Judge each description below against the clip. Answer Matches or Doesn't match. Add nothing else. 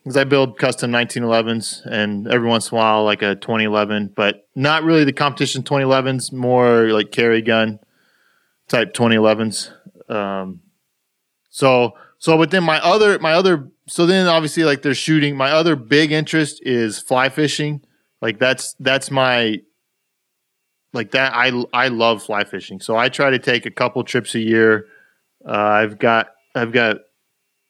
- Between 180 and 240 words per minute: Doesn't match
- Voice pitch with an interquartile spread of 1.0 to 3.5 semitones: Doesn't match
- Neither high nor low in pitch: Doesn't match